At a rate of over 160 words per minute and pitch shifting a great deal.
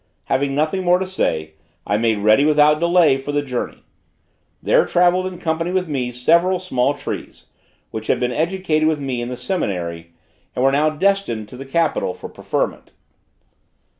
Yes: average, 170 wpm; wide, 6.0 semitones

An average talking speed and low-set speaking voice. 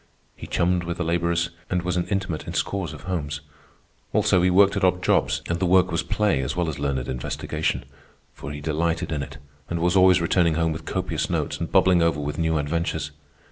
No: fast, 215 wpm; very low, 85 Hz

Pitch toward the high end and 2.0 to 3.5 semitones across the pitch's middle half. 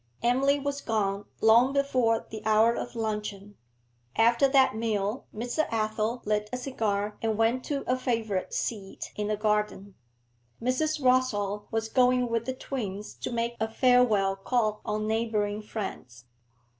Yes: high, 225 Hz; average, 3.0 semitones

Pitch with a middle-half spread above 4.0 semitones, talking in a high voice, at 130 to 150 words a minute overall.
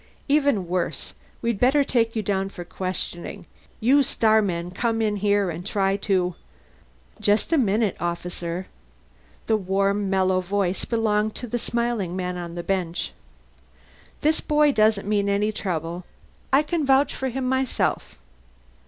Yes: average, 4.4 semitones; high, 205 Hz; average, 145 wpm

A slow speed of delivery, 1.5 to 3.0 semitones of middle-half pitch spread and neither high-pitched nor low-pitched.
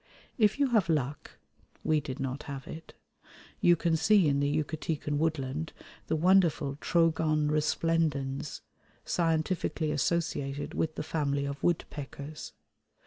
Yes: slow, 125 wpm; narrow, 2.6 semitones; medium, 155 Hz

